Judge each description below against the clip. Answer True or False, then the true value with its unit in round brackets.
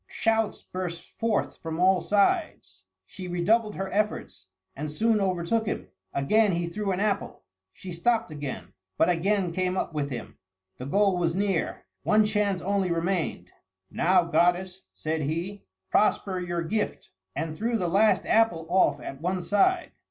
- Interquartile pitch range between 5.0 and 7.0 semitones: False (3.7 semitones)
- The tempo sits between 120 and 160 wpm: True (155 wpm)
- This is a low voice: False (185 Hz)